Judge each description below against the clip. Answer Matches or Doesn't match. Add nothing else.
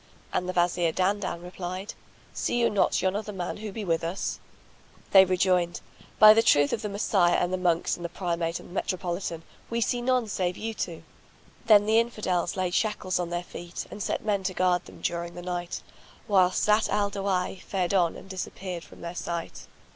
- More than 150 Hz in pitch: Matches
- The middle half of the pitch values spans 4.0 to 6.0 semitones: Doesn't match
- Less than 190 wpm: Doesn't match